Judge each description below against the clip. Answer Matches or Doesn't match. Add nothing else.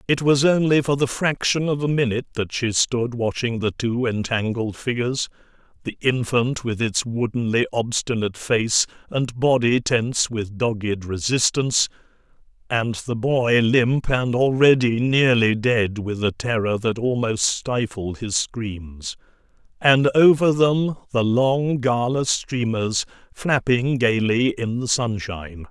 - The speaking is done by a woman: Doesn't match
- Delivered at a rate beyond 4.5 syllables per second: Doesn't match